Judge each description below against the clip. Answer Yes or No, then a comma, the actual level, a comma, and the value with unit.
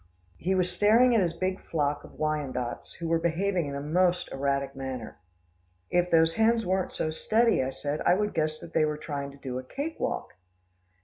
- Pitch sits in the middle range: Yes, medium, 165 Hz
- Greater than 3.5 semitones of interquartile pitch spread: Yes, average, 4.8 semitones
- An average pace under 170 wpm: No, average, 200 wpm